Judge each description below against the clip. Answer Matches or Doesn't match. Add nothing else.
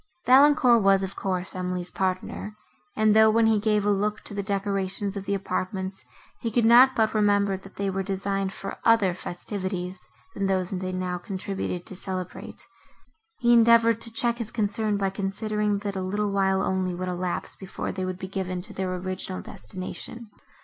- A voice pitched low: Doesn't match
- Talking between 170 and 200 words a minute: Matches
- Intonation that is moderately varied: Doesn't match